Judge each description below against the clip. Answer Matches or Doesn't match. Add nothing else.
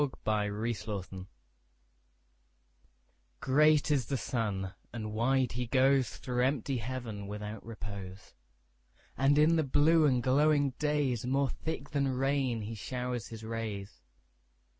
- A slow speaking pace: Matches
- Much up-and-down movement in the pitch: Doesn't match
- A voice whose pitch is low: Matches